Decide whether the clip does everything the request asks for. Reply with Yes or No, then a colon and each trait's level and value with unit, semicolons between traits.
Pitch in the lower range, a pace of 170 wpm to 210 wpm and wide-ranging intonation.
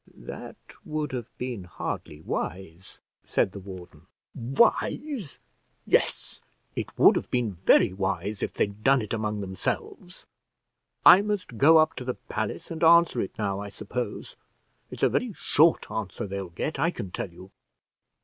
No: low, 110 Hz; average, 155 wpm; wide, 7.8 semitones